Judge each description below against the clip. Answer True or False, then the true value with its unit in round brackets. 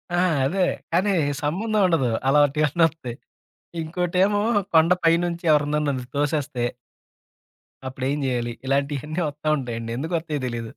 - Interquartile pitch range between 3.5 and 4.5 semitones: True (4.1 semitones)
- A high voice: False (150 Hz)